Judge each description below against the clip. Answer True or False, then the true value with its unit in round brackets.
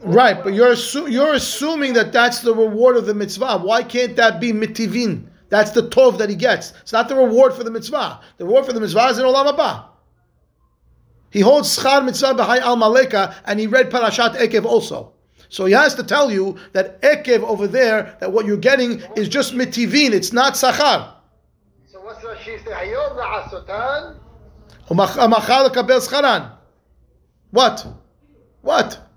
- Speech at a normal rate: True (165 wpm)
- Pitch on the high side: True (240 Hz)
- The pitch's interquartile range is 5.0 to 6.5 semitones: False (3.3 semitones)